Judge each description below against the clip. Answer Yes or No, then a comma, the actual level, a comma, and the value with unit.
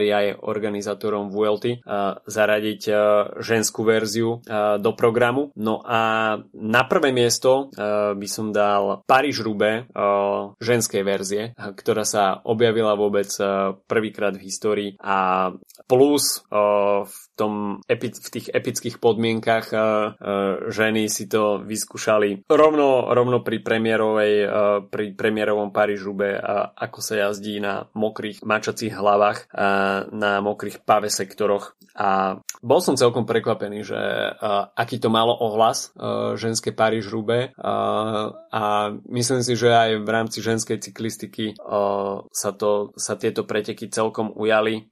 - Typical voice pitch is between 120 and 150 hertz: No, low, 105 Hz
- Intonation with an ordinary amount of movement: No, narrow, 1.7 semitones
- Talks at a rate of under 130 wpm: Yes, average, 120 wpm